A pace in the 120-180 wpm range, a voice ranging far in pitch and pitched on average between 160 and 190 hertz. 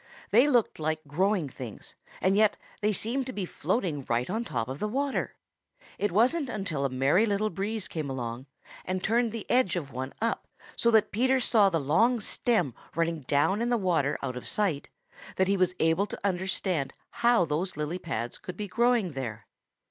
No: average, 190 wpm; wide, 7.1 semitones; medium, 185 Hz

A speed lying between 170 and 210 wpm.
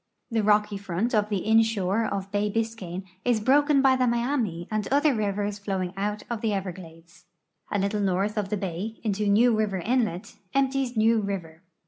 Yes: average, 175 wpm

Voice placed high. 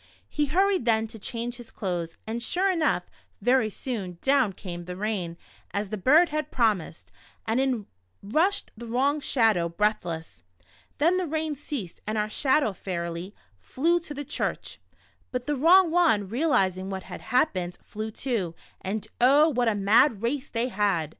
Yes: high, 230 Hz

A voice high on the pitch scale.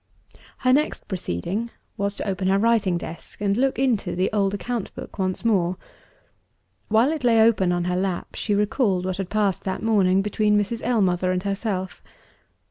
Yes: high, 200 Hz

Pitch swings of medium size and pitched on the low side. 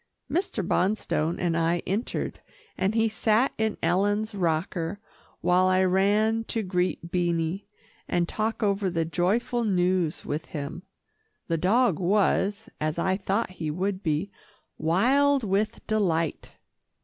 No: average, 3.9 semitones; high, 190 Hz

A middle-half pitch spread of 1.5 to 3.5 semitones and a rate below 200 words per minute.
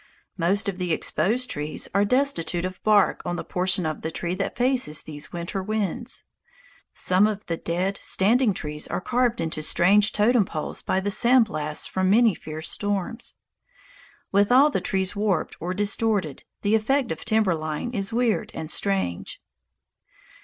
No: average, 4.3 semitones; average, 165 wpm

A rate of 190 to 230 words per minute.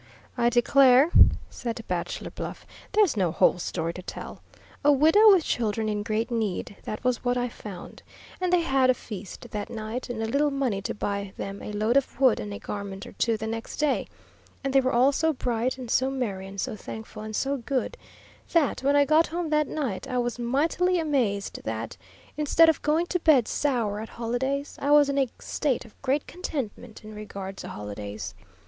Yes: average, 200 wpm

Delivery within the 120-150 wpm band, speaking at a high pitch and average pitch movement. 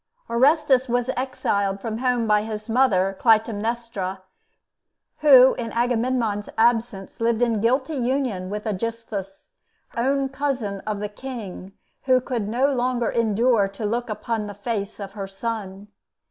Yes: average, 140 wpm; high, 230 Hz; average, 3.4 semitones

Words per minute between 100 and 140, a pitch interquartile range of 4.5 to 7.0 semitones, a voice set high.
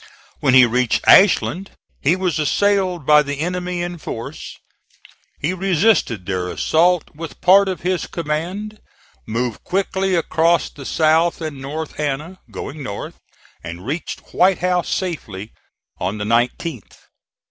No: slow, 135 wpm; wide, 5.4 semitones; medium, 160 Hz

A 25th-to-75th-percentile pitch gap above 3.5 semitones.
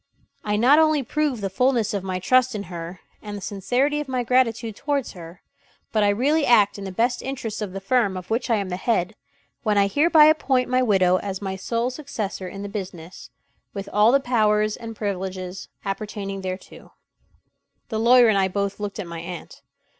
Yes: average, 4.5 semitones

